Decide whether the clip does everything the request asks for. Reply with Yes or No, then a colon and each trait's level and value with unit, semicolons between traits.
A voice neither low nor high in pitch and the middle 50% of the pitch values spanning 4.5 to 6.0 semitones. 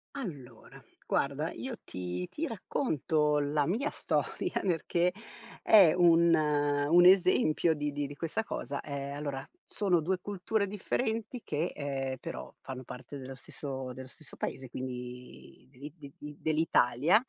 Yes: medium, 150 Hz; average, 4.9 semitones